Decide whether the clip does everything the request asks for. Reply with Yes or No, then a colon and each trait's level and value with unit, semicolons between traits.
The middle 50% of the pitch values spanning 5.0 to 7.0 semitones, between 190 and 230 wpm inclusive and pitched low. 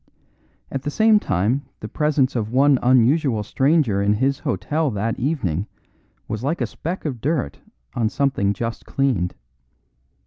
No: average, 5.3 semitones; average, 145 wpm; low, 130 Hz